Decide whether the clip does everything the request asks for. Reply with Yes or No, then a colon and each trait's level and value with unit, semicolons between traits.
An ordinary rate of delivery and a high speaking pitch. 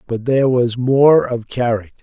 No: average, 180 wpm; low, 125 Hz